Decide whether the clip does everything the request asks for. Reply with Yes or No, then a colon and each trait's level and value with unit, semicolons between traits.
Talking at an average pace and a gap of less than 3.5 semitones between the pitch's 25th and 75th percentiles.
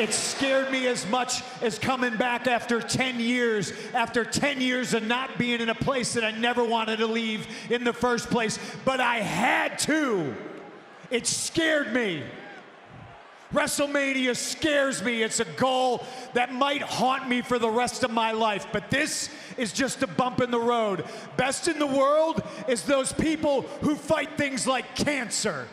Yes: average, 175 wpm; narrow, 2.4 semitones